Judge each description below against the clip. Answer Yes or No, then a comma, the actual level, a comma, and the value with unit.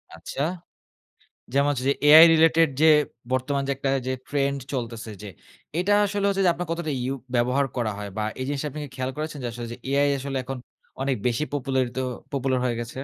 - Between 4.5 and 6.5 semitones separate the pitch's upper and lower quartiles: No, average, 3.1 semitones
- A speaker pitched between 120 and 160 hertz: Yes, medium, 140 Hz